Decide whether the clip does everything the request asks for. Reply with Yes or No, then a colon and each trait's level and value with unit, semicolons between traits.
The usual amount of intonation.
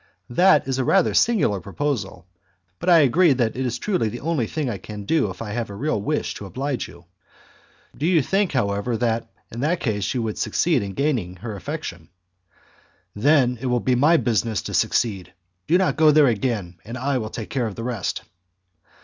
No: wide, 5.9 semitones